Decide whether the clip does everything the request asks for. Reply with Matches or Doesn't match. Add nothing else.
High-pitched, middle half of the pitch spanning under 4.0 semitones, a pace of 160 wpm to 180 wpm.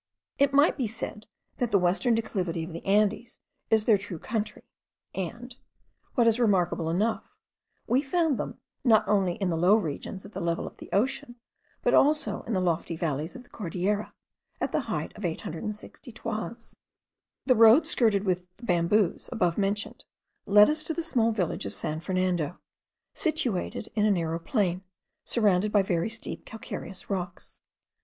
Doesn't match